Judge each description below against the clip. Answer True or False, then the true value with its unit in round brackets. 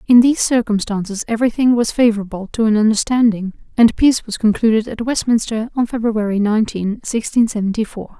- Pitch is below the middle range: False (220 Hz)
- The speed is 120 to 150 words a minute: True (145 wpm)